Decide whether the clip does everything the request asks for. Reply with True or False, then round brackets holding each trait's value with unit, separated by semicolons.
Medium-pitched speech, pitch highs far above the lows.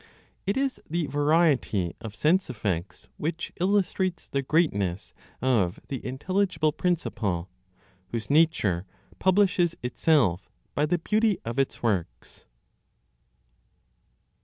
True (145 Hz; 8.6 semitones)